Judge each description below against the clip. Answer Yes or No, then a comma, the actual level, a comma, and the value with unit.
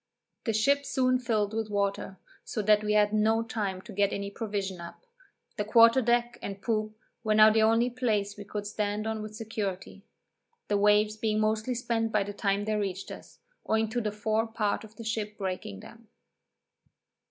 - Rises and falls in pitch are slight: Yes, narrow, 1.6 semitones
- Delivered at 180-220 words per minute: Yes, average, 185 wpm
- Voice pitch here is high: Yes, high, 215 Hz